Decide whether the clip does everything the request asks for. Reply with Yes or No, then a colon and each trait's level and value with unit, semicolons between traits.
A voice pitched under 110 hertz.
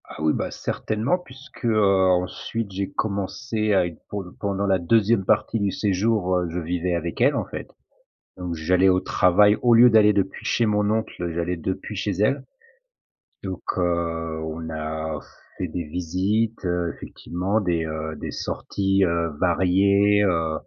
Yes: very low, 95 Hz